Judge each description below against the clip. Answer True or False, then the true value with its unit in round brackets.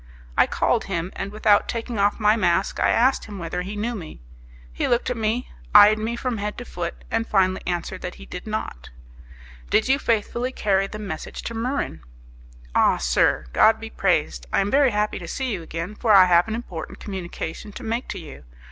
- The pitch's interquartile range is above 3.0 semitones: True (4.1 semitones)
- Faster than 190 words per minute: True (205 wpm)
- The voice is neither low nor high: False (210 Hz)